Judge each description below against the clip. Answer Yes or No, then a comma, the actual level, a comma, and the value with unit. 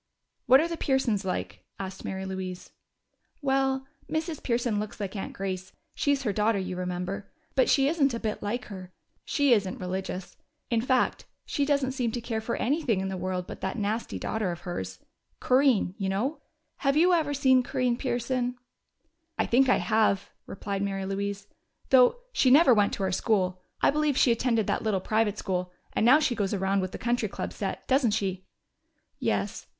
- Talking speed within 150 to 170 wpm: No, average, 185 wpm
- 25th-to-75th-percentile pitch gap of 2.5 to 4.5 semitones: No, wide, 5.4 semitones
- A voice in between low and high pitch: No, high, 220 Hz